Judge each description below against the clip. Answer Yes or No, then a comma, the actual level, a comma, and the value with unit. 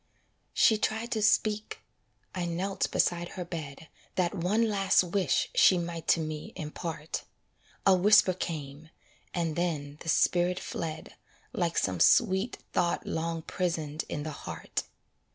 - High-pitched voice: No, medium, 175 Hz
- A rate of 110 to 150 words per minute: Yes, slow, 135 wpm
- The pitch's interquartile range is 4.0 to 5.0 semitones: No, average, 3.2 semitones